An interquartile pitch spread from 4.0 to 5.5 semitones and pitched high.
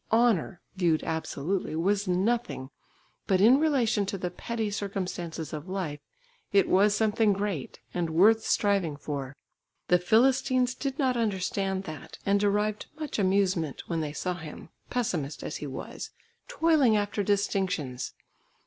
Yes: average, 4.8 semitones; high, 195 Hz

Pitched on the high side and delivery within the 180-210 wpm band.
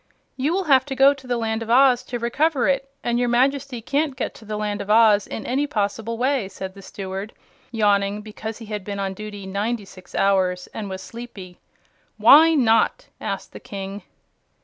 Yes: high, 225 Hz; average, 195 wpm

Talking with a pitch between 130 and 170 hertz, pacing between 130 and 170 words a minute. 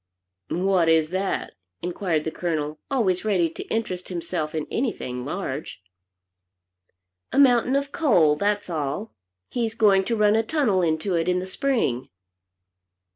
No: medium, 185 Hz; average, 140 wpm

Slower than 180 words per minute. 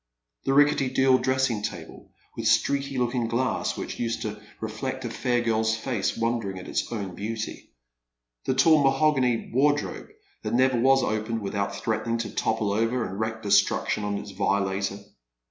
Yes: average, 165 wpm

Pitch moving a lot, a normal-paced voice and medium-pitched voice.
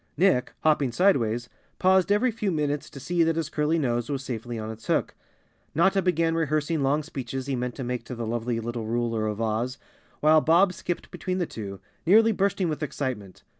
Yes: wide, 6.0 semitones; average, 195 wpm; medium, 145 Hz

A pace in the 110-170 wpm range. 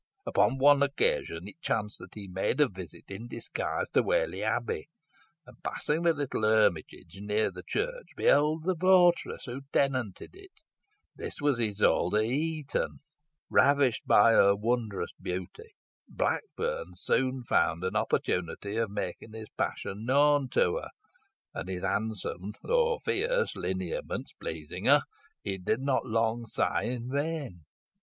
Yes: average, 140 wpm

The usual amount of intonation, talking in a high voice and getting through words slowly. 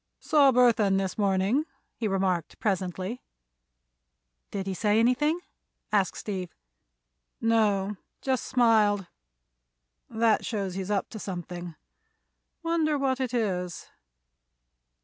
Yes: average, 4.3 semitones; high, 210 Hz; slow, 105 wpm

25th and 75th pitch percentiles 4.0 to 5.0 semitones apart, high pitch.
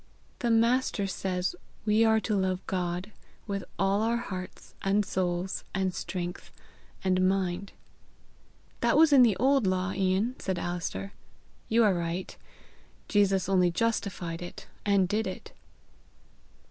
No: average, 3.0 semitones; high, 195 Hz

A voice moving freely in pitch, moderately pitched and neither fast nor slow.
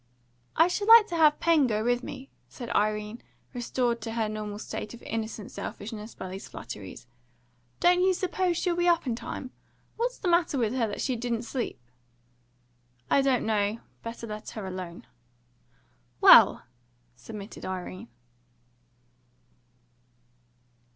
No: wide, 6.3 semitones; high, 235 Hz; average, 145 wpm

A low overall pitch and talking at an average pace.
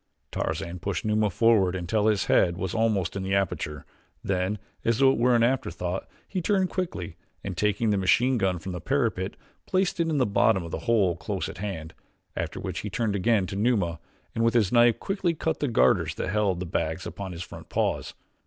No: low, 100 Hz; fast, 210 wpm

